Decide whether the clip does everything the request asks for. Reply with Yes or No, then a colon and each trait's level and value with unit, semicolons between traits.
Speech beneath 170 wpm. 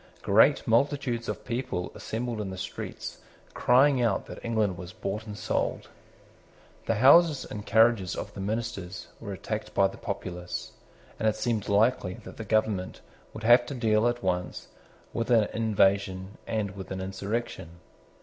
Yes: average, 160 wpm